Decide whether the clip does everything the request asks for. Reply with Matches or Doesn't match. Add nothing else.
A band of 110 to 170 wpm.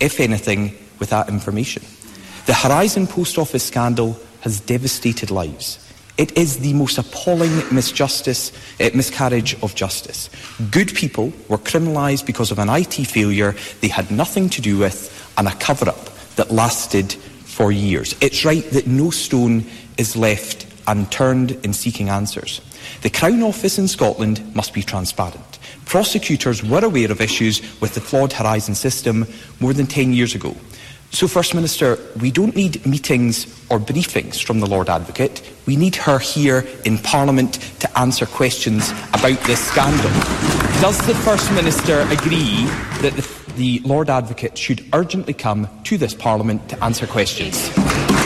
Matches